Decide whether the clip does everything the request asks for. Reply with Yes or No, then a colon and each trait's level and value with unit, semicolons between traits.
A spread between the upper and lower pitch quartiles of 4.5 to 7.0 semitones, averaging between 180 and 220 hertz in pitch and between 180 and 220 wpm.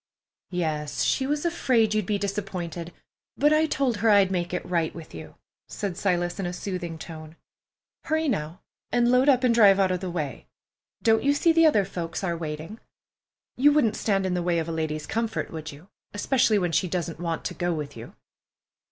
Yes: wide, 5.5 semitones; medium, 185 Hz; average, 200 wpm